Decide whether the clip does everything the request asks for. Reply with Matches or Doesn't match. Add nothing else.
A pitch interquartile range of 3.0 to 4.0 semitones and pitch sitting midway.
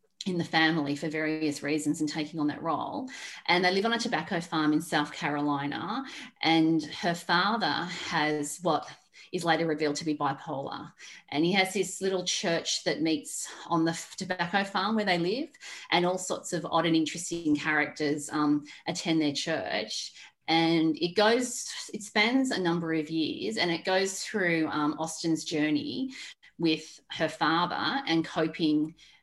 Matches